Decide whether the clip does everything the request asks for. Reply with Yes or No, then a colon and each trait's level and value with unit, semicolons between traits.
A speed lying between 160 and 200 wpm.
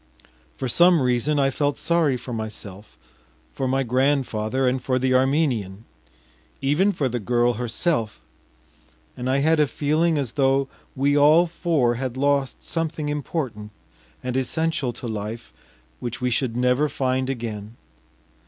No: average, 145 wpm